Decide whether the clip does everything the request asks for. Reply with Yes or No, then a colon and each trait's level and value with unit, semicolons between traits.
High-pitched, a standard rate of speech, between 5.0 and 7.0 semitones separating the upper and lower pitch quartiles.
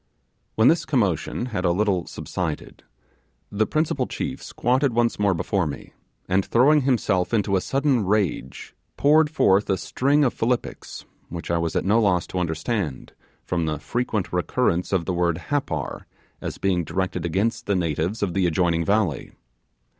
No: very low, 95 Hz; average, 160 wpm; wide, 5.6 semitones